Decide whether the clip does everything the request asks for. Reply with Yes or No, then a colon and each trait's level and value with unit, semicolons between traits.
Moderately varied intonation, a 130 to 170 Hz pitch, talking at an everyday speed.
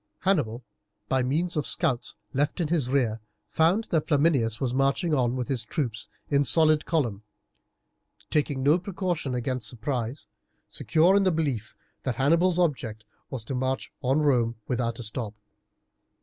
Yes: average, 4.8 semitones; low, 135 Hz; average, 150 wpm